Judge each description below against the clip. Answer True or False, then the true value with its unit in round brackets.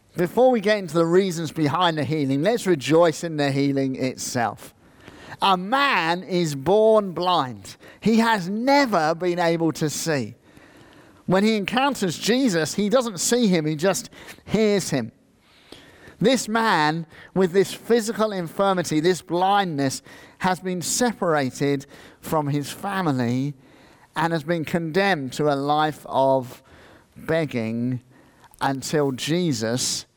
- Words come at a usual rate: False (125 wpm)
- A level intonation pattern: False (5.6 semitones)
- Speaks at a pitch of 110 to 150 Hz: False (165 Hz)